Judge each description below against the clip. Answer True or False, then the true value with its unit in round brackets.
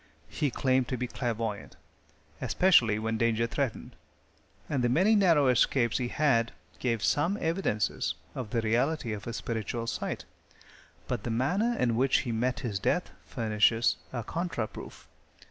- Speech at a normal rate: True (150 wpm)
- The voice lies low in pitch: True (120 Hz)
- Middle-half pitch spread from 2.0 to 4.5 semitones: True (3.8 semitones)